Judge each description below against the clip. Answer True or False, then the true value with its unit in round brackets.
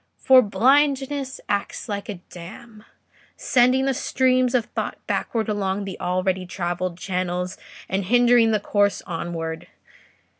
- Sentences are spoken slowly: True (125 wpm)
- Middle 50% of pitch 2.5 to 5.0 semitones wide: False (5.5 semitones)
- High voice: True (205 Hz)